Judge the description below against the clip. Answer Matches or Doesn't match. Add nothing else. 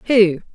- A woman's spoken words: Matches